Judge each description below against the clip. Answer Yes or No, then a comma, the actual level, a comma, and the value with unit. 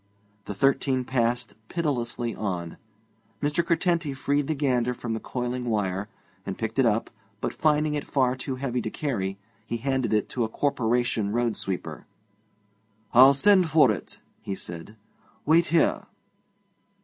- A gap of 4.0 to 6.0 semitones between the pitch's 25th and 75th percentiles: Yes, average, 4.3 semitones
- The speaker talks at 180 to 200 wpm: No, average, 150 wpm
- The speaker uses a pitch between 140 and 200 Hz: No, low, 125 Hz